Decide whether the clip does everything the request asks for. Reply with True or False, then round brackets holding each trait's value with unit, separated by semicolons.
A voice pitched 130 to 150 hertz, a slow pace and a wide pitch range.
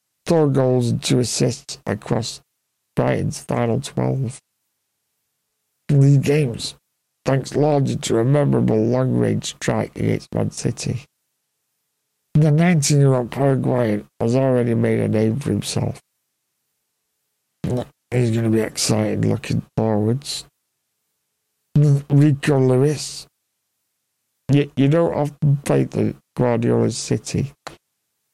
False (135 Hz; 110 wpm; 3.8 semitones)